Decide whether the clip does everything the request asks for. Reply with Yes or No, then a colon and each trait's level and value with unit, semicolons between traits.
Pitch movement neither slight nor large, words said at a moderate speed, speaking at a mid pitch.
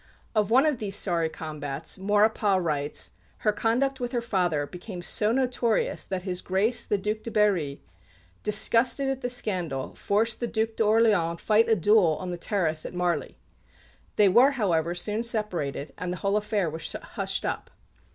No: average, 4.4 semitones; average, 170 wpm; high, 205 Hz